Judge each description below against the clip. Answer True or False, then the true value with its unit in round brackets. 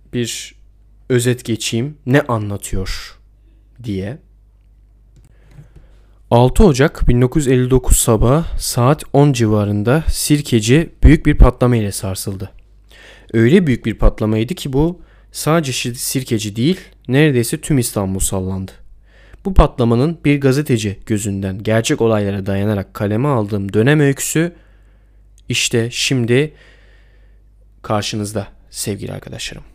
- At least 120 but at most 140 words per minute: False (100 wpm)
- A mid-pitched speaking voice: False (115 Hz)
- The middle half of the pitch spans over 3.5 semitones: True (4.6 semitones)